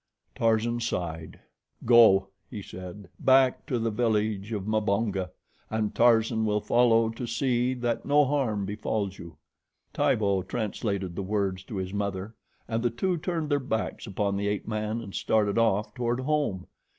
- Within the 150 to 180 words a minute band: Yes, average, 155 wpm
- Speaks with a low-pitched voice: Yes, low, 110 Hz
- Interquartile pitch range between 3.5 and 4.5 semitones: No, average, 3.0 semitones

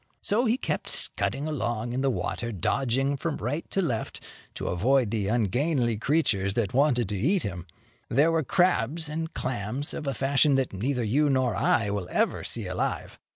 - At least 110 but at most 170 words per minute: No, average, 180 wpm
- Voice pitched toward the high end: No, low, 130 Hz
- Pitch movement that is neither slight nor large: Yes, average, 5.0 semitones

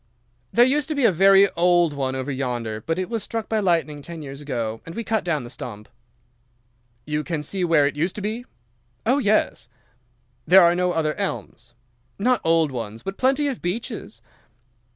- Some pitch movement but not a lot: No, wide, 6.9 semitones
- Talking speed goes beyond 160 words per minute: Yes, average, 190 wpm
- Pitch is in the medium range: Yes, medium, 170 Hz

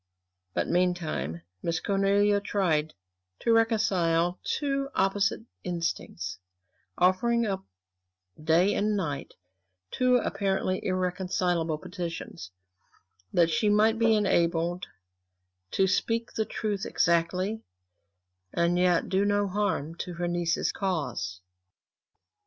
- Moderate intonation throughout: Yes, average, 3.4 semitones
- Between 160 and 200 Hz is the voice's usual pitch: Yes, medium, 185 Hz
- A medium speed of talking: No, slow, 100 wpm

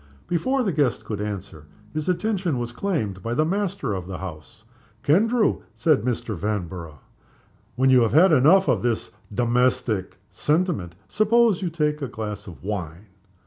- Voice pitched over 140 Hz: No, low, 125 Hz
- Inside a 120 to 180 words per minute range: Yes, average, 150 wpm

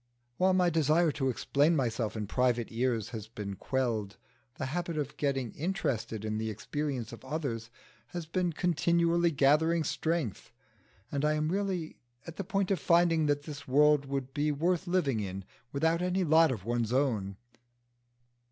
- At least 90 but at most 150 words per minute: No, average, 160 wpm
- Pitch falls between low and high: Yes, medium, 145 Hz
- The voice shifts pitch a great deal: Yes, wide, 5.9 semitones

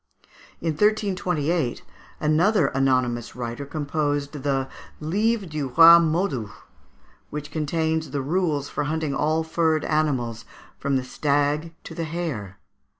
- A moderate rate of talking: No, slow, 120 wpm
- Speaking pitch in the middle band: Yes, medium, 150 Hz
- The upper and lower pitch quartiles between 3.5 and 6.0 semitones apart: No, average, 3.0 semitones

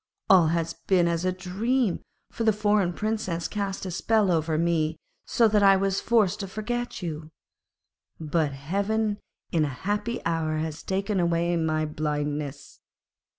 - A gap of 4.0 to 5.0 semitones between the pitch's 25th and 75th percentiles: Yes, average, 4.5 semitones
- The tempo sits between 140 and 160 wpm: Yes, average, 150 wpm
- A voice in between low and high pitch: Yes, medium, 180 Hz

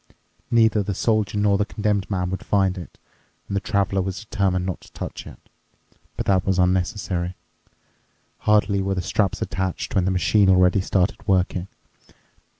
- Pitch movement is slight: Yes, narrow, 1.8 semitones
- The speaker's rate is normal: Yes, average, 160 wpm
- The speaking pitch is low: Yes, very low, 95 Hz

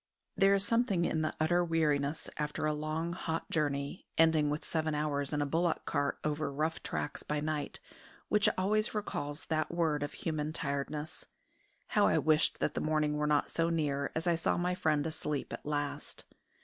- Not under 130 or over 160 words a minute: No, average, 185 wpm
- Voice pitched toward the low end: No, medium, 155 Hz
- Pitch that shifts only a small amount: Yes, narrow, 1.9 semitones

